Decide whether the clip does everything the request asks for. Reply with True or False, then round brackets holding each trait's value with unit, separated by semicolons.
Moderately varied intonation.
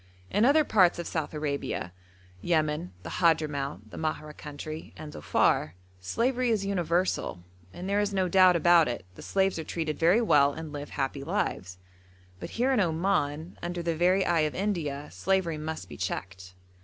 True (4.3 semitones)